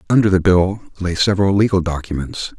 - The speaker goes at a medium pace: Yes, average, 160 wpm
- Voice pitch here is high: No, very low, 95 Hz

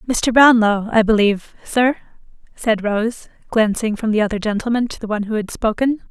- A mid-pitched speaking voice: No, high, 220 Hz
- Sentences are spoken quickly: No, average, 175 wpm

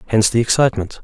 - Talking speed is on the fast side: No, average, 175 wpm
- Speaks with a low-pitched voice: Yes, low, 110 Hz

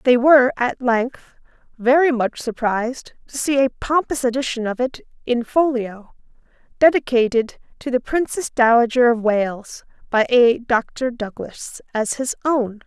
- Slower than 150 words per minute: Yes, average, 140 wpm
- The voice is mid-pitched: No, high, 245 Hz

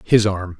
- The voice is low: Yes, low, 100 Hz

